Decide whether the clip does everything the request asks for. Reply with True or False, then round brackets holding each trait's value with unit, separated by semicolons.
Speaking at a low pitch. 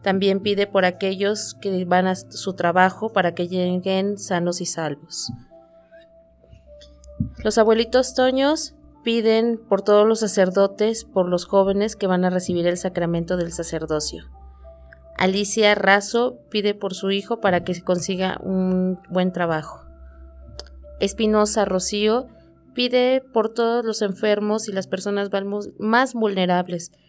False (190 Hz)